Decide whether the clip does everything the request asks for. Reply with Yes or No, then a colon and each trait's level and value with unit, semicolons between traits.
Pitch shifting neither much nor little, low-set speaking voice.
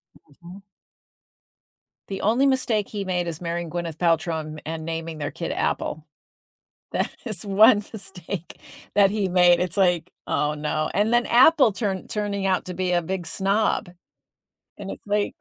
No: average, 3.6 semitones; medium, 185 Hz